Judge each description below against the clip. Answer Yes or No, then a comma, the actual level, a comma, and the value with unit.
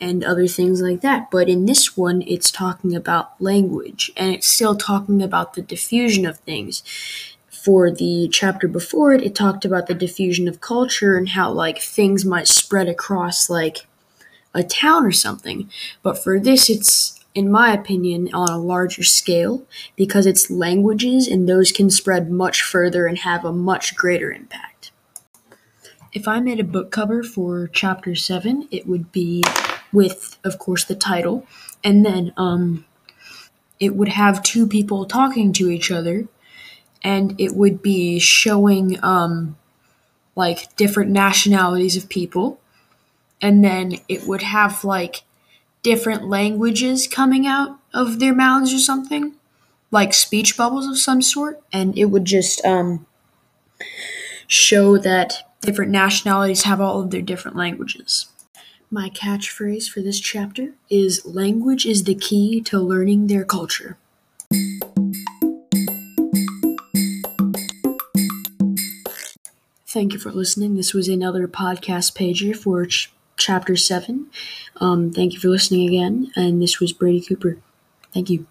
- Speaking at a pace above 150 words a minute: No, average, 145 wpm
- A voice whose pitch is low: No, high, 195 Hz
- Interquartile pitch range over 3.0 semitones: No, narrow, 2.6 semitones